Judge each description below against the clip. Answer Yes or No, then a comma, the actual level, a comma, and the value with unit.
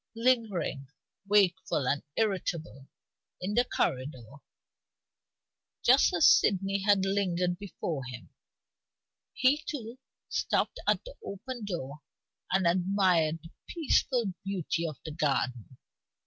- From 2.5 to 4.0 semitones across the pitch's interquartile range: No, average, 5.2 semitones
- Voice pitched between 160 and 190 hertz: Yes, medium, 185 Hz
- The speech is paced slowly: Yes, slow, 105 wpm